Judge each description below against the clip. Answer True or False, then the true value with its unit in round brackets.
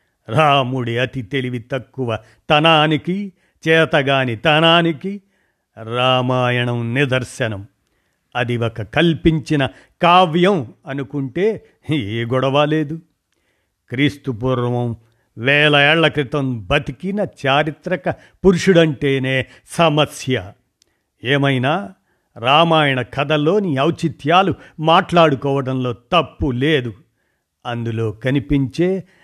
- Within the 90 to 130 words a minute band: False (70 wpm)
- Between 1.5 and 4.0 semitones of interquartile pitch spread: False (4.4 semitones)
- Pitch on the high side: False (140 Hz)